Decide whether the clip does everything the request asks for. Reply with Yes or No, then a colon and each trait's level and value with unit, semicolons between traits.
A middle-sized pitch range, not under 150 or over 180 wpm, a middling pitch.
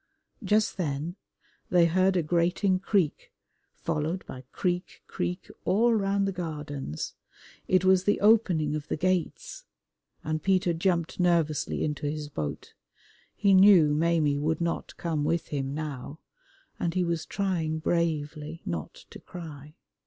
No: average, 3.5 semitones; average, 140 wpm; medium, 170 Hz